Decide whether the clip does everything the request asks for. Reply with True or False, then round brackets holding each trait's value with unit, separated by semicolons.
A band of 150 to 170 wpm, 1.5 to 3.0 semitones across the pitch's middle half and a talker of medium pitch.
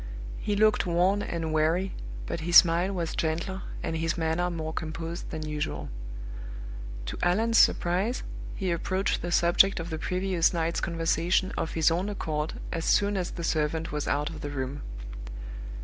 True (165 wpm; 2.6 semitones; 170 Hz)